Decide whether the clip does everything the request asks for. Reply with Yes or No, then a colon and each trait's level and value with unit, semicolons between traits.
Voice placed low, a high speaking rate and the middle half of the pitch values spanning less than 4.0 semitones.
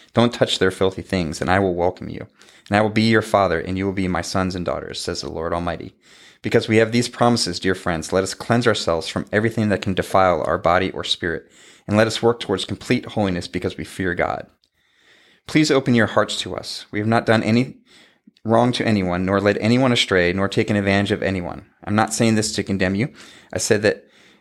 Yes: low, 100 Hz; fast, 225 wpm; average, 3.5 semitones